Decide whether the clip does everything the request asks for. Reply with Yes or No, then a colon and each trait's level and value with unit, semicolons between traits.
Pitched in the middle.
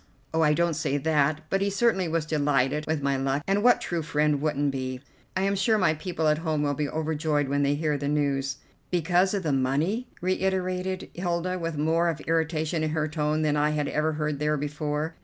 Yes: medium, 155 Hz